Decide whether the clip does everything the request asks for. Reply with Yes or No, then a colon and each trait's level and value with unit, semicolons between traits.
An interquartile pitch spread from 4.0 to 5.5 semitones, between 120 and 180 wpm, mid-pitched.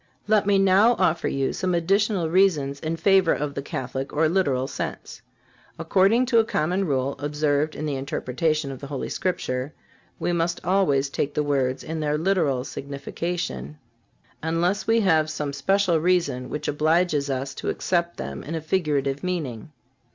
Yes: average, 4.7 semitones; average, 165 wpm; medium, 155 Hz